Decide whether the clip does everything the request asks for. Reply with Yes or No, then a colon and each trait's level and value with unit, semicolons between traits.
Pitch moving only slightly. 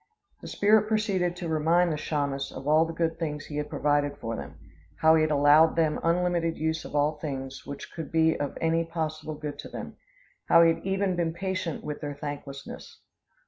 Yes: narrow, 2.3 semitones